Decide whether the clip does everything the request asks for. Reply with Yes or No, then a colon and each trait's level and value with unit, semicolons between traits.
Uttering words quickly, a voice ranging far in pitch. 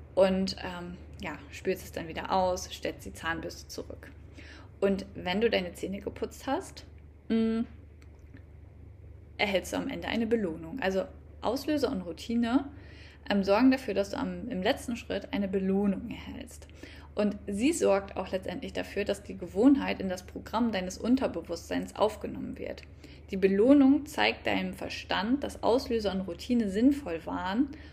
No: average, 150 wpm; wide, 6.2 semitones